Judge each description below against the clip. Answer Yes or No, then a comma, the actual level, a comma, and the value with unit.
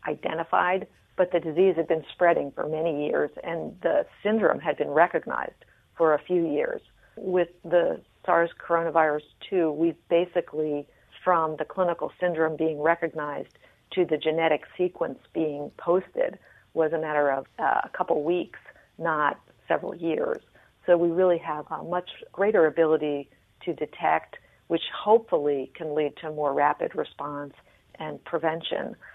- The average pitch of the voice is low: No, medium, 165 Hz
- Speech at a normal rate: Yes, average, 145 wpm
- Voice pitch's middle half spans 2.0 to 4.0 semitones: Yes, narrow, 2.6 semitones